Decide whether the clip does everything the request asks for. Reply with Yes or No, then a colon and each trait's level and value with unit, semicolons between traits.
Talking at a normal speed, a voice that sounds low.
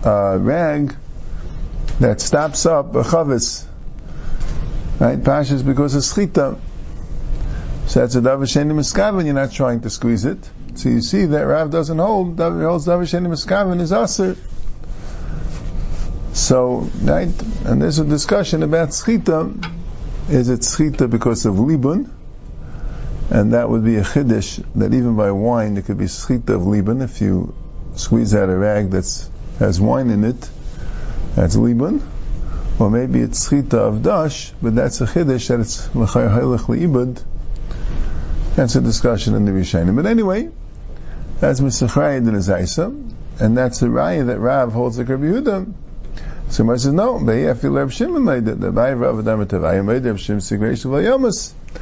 Yes: average, 155 wpm; low, 125 Hz